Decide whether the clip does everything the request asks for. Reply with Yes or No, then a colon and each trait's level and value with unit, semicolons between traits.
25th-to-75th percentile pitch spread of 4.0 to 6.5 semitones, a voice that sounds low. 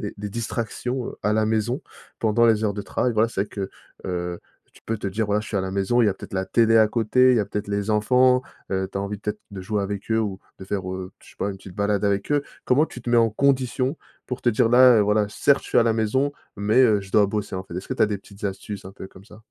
No: average, 2.8 semitones; low, 105 Hz